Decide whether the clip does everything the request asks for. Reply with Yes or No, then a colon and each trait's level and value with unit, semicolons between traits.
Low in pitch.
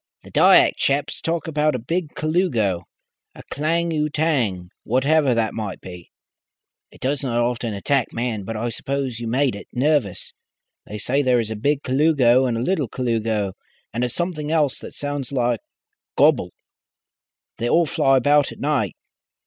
Yes: low, 130 Hz